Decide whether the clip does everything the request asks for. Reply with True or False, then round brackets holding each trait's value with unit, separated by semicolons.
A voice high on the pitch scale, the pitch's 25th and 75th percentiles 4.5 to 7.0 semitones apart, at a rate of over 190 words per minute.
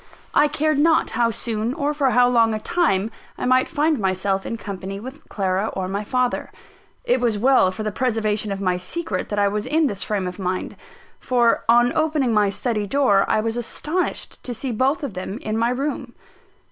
True (230 Hz; 5.0 semitones; 200 wpm)